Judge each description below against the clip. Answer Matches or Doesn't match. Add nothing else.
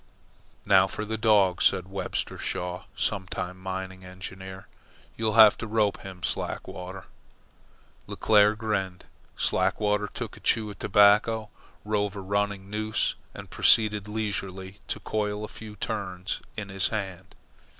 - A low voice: Matches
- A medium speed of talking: Doesn't match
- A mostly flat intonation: Matches